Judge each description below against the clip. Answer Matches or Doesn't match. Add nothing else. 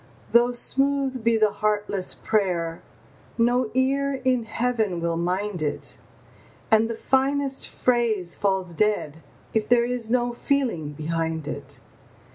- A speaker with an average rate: Doesn't match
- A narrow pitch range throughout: Doesn't match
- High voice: Matches